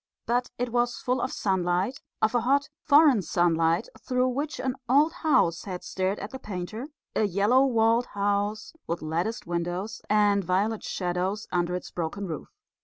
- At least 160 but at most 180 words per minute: Yes, average, 165 wpm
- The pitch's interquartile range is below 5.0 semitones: No, wide, 5.5 semitones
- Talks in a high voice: Yes, high, 205 Hz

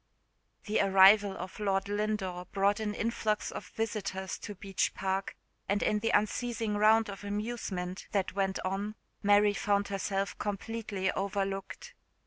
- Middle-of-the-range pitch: No, high, 200 Hz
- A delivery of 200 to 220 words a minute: No, slow, 135 wpm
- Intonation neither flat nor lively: No, narrow, 1.5 semitones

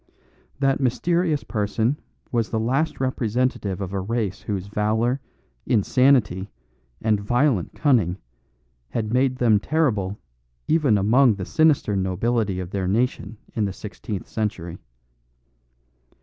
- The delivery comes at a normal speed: No, slow, 120 wpm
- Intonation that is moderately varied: Yes, average, 4.4 semitones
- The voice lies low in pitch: Yes, low, 110 Hz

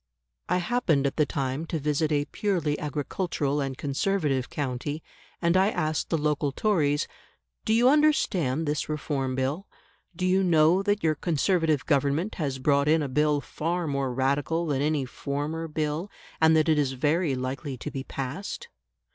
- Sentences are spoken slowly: No, average, 165 wpm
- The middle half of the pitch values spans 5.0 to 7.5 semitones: No, average, 3.2 semitones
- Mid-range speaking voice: Yes, medium, 150 Hz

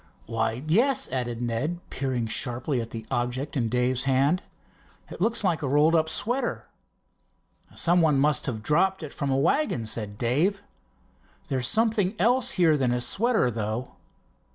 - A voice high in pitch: No, medium, 140 Hz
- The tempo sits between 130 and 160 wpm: Yes, average, 155 wpm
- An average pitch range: No, wide, 6.7 semitones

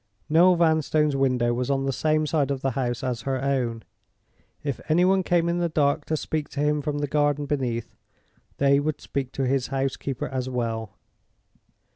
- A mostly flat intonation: No, average, 3.0 semitones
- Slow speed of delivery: No, average, 185 wpm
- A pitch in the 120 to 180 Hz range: Yes, medium, 140 Hz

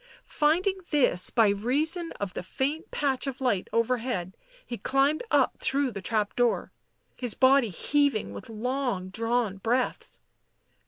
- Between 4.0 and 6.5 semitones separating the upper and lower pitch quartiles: Yes, average, 4.5 semitones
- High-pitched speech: Yes, very high, 250 Hz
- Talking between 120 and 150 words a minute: Yes, average, 140 wpm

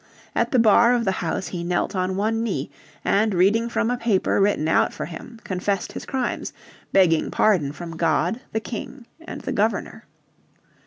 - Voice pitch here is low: No, high, 200 Hz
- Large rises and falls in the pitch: No, average, 4.6 semitones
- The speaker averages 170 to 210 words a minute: Yes, average, 175 wpm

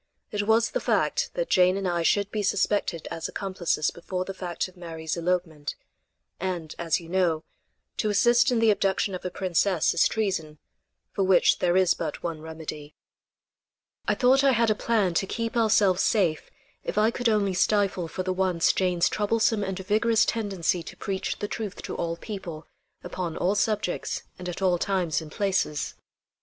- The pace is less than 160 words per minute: No, average, 180 wpm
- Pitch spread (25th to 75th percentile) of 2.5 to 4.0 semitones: Yes, average, 3.4 semitones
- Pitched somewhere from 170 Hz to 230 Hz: Yes, high, 190 Hz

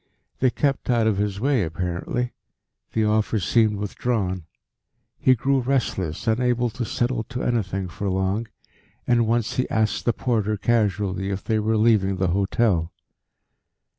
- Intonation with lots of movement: No, average, 3.7 semitones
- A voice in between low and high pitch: No, low, 110 Hz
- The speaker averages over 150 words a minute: No, average, 145 wpm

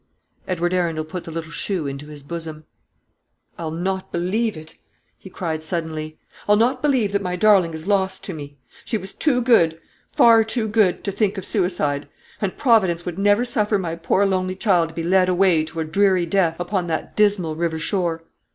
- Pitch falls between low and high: Yes, medium, 180 Hz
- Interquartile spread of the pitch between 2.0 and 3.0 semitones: No, average, 3.7 semitones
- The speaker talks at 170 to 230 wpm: Yes, average, 190 wpm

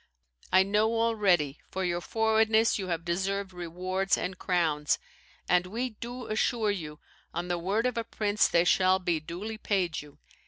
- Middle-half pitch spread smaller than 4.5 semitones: Yes, average, 3.9 semitones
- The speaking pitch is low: No, high, 190 Hz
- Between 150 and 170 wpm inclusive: Yes, average, 165 wpm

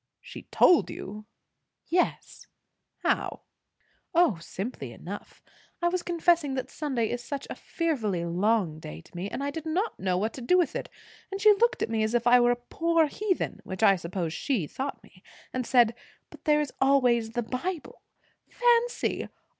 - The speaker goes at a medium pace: Yes, average, 180 wpm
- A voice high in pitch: Yes, very high, 250 Hz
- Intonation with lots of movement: Yes, wide, 8.0 semitones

